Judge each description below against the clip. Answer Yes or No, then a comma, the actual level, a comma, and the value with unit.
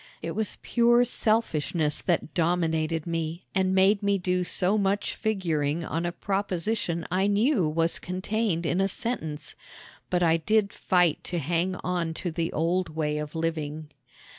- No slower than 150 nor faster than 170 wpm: Yes, average, 155 wpm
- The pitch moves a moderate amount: Yes, average, 3.3 semitones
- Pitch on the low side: No, medium, 175 Hz